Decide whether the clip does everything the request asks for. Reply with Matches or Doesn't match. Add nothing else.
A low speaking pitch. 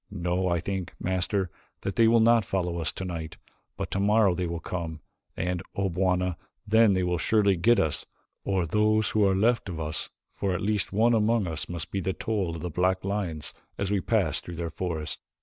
Matches